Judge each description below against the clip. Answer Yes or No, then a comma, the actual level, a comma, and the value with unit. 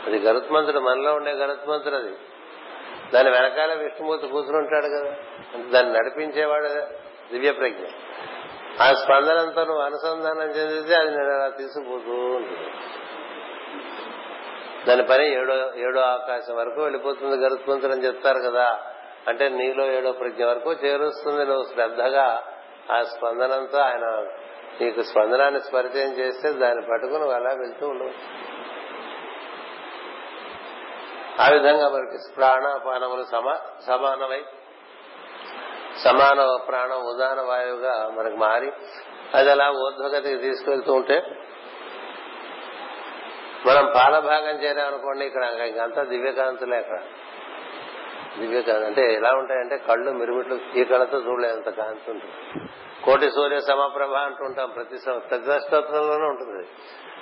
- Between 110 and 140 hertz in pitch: Yes, low, 135 Hz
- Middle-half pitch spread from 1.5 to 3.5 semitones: Yes, narrow, 2.4 semitones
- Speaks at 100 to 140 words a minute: Yes, average, 105 wpm